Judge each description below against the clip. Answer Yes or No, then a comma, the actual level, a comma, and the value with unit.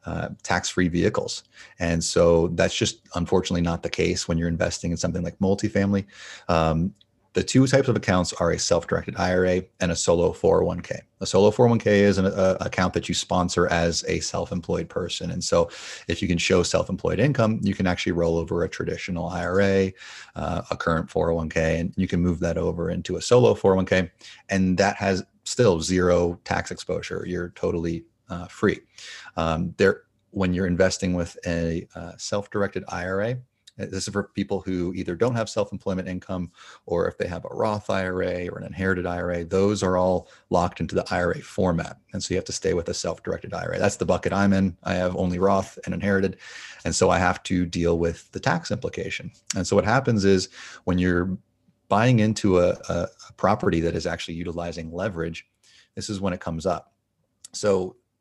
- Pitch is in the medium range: No, very low, 95 Hz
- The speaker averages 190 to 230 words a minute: Yes, average, 195 wpm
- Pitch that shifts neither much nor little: No, narrow, 2.2 semitones